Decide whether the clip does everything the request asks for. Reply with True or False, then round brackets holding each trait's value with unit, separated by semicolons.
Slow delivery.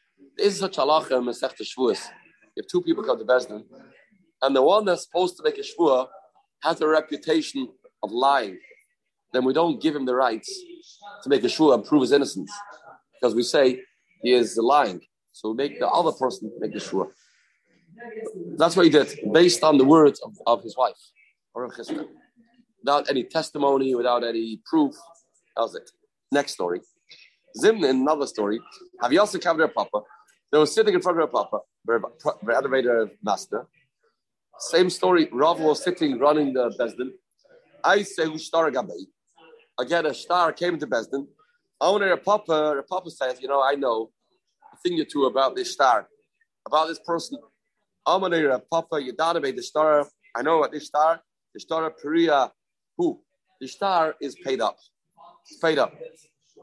False (165 wpm)